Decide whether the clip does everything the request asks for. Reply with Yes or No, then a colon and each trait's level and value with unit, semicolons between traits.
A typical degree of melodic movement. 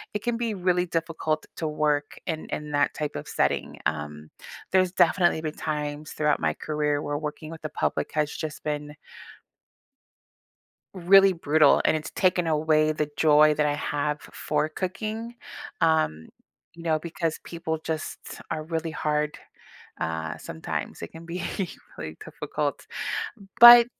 No: narrow, 2.3 semitones